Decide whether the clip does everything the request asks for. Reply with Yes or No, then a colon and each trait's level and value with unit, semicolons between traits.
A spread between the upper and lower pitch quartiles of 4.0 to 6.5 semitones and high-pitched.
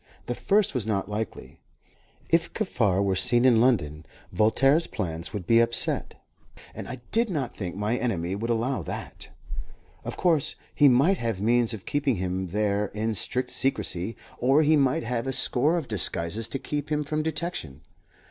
No: wide, 5.4 semitones; low, 120 Hz